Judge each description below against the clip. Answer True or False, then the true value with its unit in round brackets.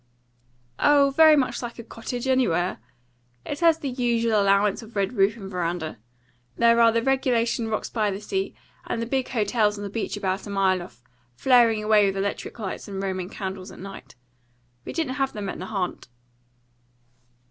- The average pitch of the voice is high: True (215 Hz)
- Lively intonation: False (4.0 semitones)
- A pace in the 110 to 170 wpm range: False (180 wpm)